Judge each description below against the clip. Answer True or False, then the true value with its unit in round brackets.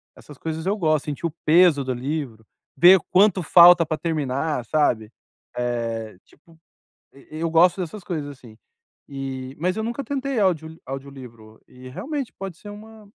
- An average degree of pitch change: False (5.7 semitones)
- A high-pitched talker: False (155 Hz)